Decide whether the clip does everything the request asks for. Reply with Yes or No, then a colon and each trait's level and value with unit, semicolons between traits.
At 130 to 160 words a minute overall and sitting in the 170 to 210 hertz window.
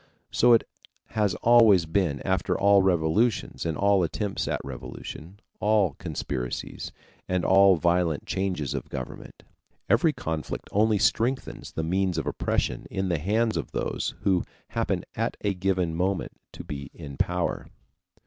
No: average, 145 wpm; very low, 95 Hz